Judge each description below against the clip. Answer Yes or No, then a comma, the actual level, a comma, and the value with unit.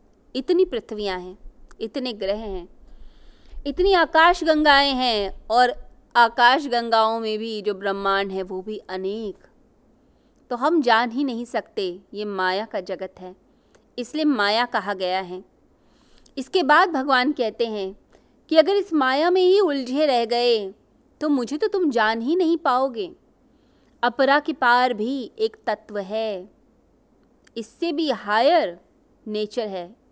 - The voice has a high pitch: Yes, high, 240 Hz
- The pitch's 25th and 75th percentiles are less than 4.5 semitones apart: No, wide, 5.6 semitones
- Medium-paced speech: Yes, average, 140 wpm